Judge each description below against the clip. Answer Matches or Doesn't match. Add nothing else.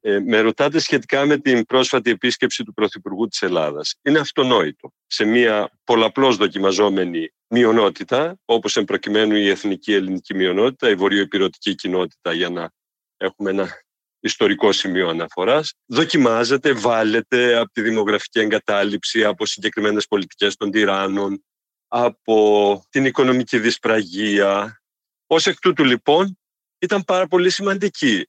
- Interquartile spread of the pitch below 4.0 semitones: Doesn't match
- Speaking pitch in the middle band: Doesn't match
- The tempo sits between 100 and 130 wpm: Matches